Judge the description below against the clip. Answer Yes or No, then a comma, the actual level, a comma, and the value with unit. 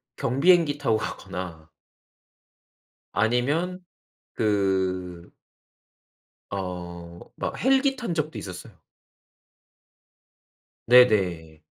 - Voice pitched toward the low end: Yes, low, 105 Hz